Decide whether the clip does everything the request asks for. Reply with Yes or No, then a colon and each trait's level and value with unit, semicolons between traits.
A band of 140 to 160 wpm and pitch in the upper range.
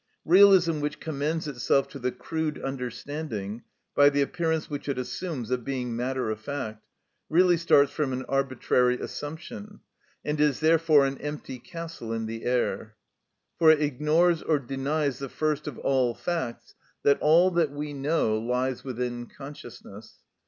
No: average, 150 wpm; medium, 140 Hz